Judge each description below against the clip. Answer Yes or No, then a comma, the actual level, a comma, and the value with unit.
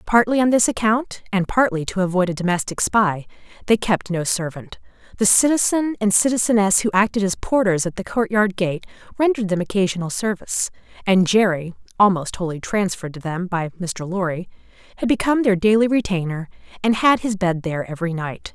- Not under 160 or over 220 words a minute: Yes, average, 170 wpm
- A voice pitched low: No, high, 195 Hz